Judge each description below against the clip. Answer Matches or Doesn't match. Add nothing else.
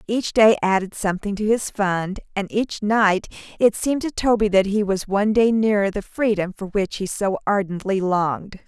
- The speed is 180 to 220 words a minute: Matches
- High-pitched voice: Matches